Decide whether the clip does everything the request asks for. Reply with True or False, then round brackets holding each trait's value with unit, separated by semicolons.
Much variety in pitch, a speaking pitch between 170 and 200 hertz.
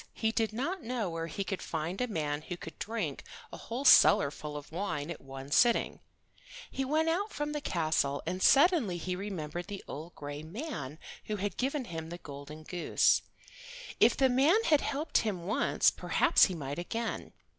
True (8.1 semitones; 185 Hz)